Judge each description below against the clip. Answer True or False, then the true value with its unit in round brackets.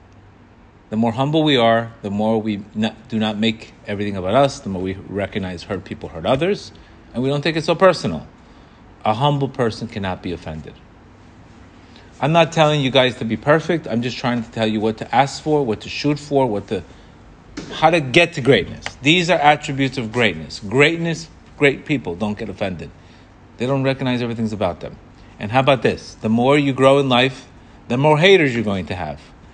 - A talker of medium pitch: False (120 Hz)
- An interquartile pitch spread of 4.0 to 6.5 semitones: True (5.2 semitones)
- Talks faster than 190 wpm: True (200 wpm)